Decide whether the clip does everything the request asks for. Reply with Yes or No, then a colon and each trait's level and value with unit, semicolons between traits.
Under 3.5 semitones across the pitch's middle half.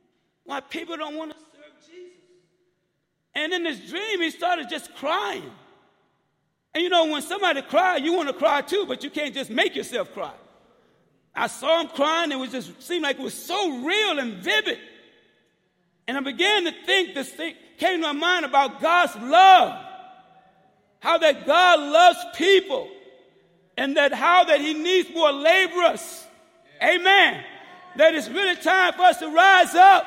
No: average, 4.1 semitones